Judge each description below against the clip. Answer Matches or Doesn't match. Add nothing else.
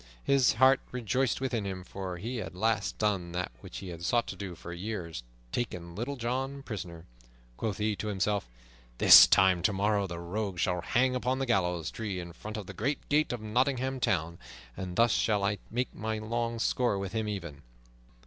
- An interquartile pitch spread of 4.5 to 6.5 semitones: Matches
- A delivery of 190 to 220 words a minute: Matches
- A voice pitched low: Matches